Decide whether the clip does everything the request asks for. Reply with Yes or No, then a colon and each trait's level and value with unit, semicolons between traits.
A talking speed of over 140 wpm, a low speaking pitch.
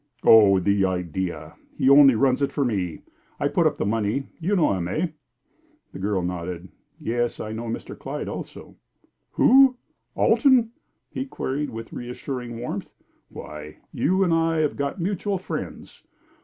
Yes: average, 155 wpm; low, 120 Hz